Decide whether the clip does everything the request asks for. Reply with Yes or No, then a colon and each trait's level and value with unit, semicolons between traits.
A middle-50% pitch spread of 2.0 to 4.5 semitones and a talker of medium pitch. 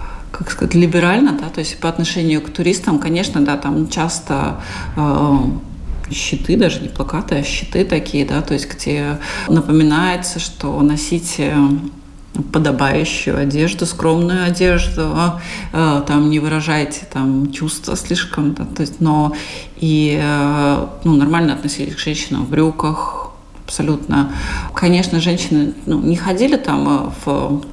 Yes: average, 2.9 semitones; medium, 155 Hz